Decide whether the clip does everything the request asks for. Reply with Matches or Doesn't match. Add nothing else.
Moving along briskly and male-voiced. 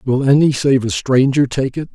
Matches